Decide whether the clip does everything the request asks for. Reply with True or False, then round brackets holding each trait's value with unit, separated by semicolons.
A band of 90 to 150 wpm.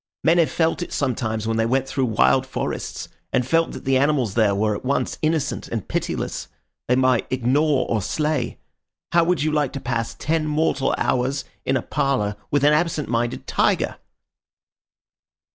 False (175 wpm)